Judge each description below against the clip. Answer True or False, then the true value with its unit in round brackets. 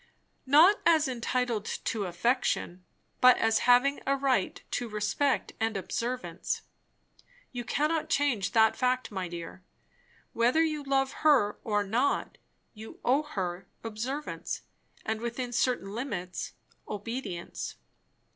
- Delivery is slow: True (120 wpm)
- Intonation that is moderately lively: True (4.6 semitones)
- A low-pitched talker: False (240 Hz)